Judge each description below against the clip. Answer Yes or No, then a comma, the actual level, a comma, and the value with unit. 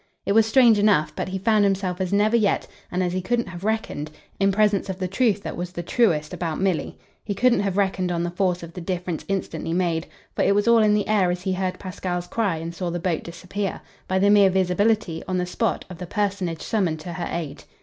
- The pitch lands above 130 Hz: Yes, medium, 185 Hz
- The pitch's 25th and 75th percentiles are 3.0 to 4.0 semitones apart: No, narrow, 2.6 semitones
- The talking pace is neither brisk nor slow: No, fast, 240 wpm